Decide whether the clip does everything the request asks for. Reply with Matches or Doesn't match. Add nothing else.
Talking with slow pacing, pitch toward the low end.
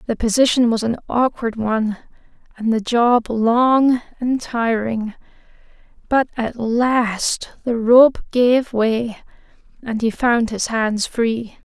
Doesn't match